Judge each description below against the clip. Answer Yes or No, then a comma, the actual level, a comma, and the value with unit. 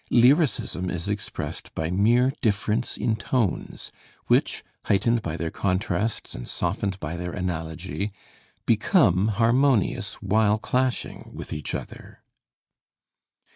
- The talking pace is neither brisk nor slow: No, slow, 110 wpm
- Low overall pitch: Yes, low, 100 Hz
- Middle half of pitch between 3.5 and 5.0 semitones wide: Yes, average, 4.7 semitones